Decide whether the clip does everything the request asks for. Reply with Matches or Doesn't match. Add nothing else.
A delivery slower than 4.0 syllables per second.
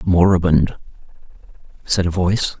Doesn't match